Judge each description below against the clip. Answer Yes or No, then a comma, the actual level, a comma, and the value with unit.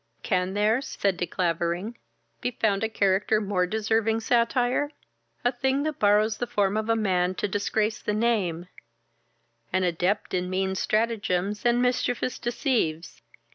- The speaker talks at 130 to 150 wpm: Yes, average, 140 wpm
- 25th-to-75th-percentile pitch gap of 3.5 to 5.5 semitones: Yes, average, 3.8 semitones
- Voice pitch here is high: Yes, high, 210 Hz